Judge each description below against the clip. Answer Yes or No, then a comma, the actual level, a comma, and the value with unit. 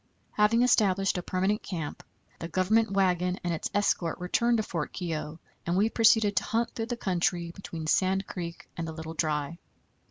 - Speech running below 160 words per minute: No, average, 180 wpm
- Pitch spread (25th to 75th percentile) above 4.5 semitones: No, average, 3.9 semitones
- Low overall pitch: No, medium, 185 Hz